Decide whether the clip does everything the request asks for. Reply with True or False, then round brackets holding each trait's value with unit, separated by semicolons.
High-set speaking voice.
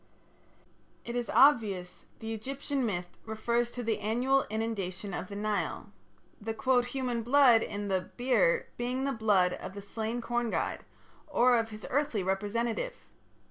True (225 Hz)